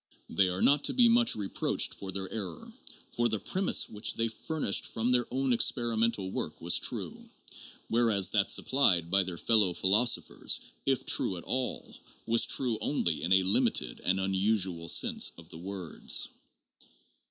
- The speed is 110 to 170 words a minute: Yes, average, 160 wpm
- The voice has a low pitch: Yes, low, 100 Hz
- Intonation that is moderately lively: Yes, average, 4.3 semitones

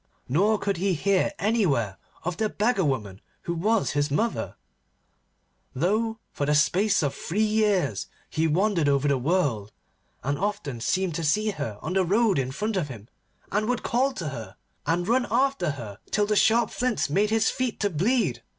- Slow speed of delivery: No, average, 180 wpm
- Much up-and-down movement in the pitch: Yes, wide, 7.0 semitones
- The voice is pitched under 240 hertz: Yes, medium, 185 Hz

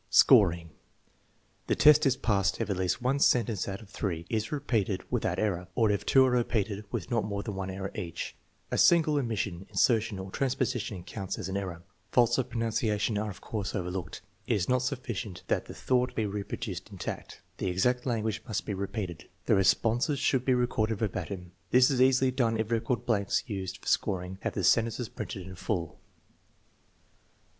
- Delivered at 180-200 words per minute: Yes, average, 185 wpm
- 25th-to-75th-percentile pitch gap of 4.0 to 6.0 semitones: Yes, average, 4.3 semitones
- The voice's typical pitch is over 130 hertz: No, low, 110 Hz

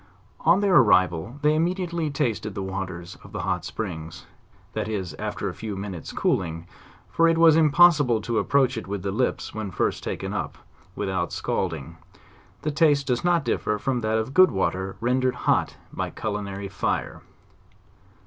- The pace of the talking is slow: No, average, 165 wpm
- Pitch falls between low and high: No, low, 110 Hz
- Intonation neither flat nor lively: No, wide, 7.6 semitones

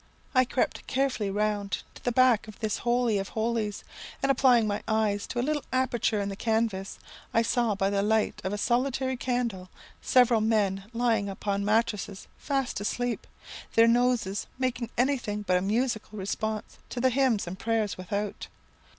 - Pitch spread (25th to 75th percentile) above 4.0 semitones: No, average, 3.2 semitones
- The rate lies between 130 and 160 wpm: No, average, 170 wpm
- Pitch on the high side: Yes, high, 220 Hz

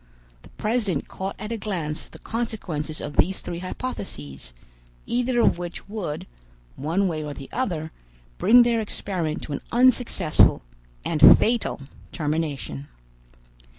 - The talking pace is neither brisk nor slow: No, slow, 130 wpm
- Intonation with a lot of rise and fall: Yes, wide, 6.6 semitones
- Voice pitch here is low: No, medium, 175 Hz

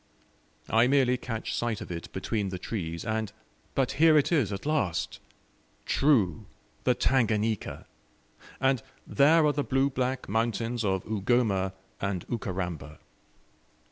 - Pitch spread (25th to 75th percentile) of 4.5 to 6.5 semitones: Yes, wide, 5.4 semitones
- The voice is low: Yes, low, 115 Hz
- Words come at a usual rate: No, slow, 130 wpm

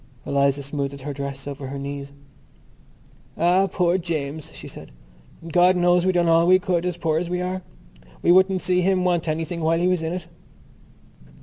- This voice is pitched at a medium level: Yes, medium, 170 Hz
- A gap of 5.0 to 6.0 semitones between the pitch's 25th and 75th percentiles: No, average, 4.2 semitones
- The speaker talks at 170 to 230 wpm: Yes, average, 180 wpm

